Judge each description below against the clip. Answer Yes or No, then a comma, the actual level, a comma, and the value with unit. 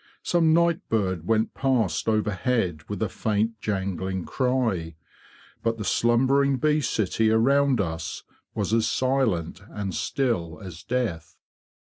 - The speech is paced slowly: Yes, slow, 125 wpm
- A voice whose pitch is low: Yes, low, 110 Hz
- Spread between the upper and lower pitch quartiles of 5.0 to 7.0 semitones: Yes, wide, 5.6 semitones